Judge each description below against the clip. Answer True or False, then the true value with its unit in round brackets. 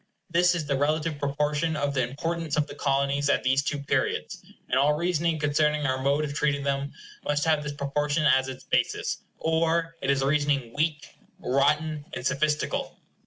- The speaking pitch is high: False (145 Hz)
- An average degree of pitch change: False (1.8 semitones)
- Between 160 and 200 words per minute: True (180 wpm)